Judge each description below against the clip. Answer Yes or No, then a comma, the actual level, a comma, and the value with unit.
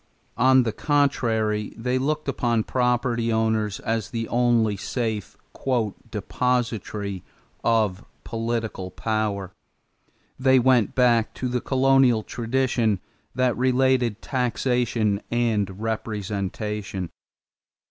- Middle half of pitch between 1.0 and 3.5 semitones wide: Yes, average, 2.8 semitones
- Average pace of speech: No, slow, 95 wpm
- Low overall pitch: Yes, low, 115 Hz